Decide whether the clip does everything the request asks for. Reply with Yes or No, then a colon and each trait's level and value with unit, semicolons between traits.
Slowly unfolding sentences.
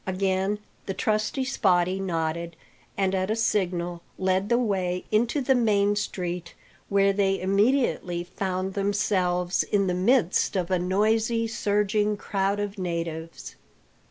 Yes: slow, 130 wpm